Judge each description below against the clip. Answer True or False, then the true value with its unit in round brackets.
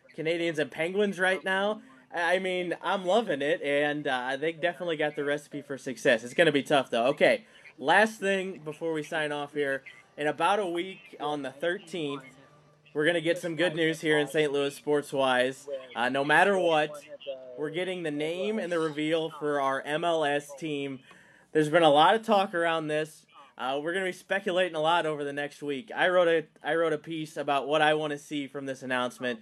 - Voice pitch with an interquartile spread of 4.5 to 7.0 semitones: False (3.2 semitones)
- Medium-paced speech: False (210 wpm)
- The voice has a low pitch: False (155 Hz)